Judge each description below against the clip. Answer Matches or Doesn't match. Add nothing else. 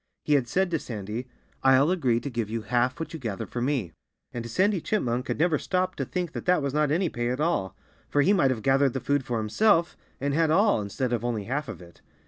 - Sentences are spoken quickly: Matches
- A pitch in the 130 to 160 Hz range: Matches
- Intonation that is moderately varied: Doesn't match